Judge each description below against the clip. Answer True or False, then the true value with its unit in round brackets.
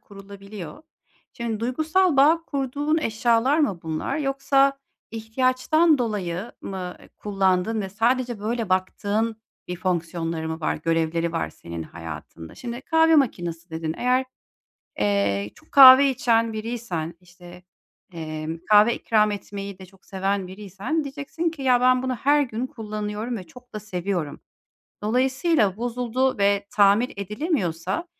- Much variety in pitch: True (6.0 semitones)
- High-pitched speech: True (215 Hz)